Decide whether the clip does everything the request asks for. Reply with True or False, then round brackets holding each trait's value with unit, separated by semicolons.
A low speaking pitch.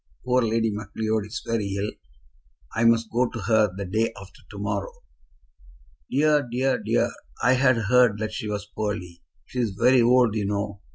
True (110 Hz)